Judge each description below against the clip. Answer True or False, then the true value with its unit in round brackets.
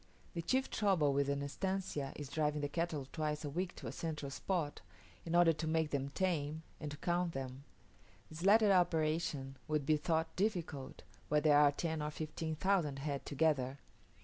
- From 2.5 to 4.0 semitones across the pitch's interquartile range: True (2.9 semitones)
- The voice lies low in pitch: False (155 Hz)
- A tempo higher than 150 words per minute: True (180 wpm)